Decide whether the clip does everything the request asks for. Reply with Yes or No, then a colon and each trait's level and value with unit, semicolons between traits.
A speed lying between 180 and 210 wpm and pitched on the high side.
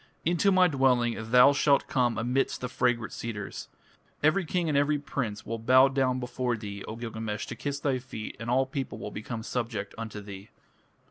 No: average, 185 wpm; low, 125 Hz